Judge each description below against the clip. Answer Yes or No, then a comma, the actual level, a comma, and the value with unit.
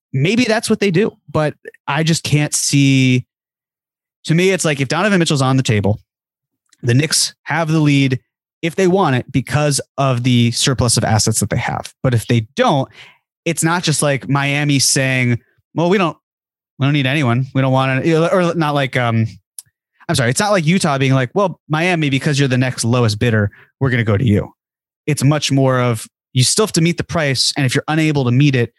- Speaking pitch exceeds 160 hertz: No, medium, 140 Hz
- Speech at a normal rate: No, fast, 215 wpm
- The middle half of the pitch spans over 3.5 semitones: Yes, average, 4.3 semitones